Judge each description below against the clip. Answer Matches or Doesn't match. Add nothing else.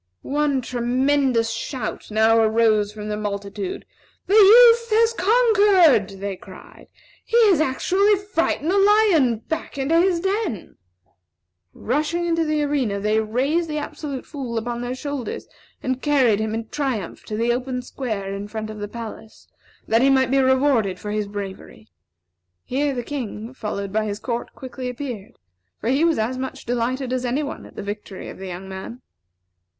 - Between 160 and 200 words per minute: Matches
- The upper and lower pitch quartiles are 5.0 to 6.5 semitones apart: Matches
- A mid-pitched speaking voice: Doesn't match